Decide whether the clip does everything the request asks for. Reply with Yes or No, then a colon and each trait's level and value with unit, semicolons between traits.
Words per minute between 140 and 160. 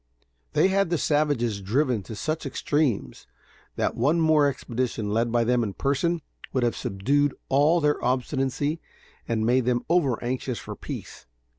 Yes: average, 155 wpm